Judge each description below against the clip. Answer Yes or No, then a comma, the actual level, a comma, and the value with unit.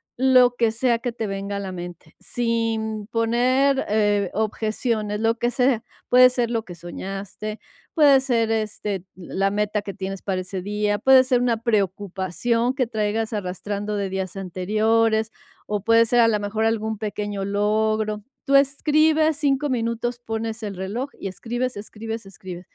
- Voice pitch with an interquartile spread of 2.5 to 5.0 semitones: Yes, average, 2.9 semitones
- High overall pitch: Yes, high, 220 Hz